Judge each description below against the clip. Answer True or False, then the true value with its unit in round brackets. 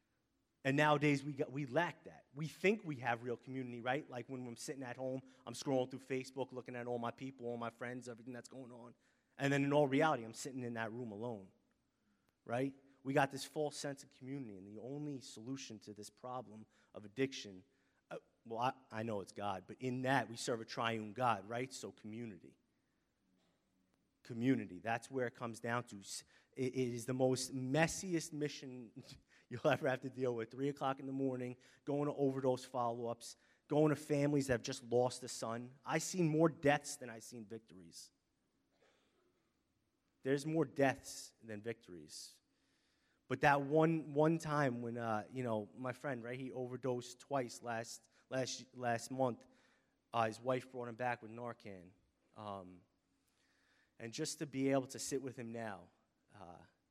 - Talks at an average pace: True (180 wpm)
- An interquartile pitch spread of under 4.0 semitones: True (2.9 semitones)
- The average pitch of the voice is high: False (125 Hz)